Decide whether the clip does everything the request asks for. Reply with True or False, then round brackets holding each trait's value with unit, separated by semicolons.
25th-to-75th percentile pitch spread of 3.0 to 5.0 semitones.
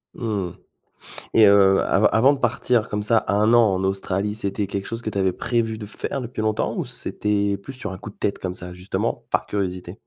False (2.4 semitones)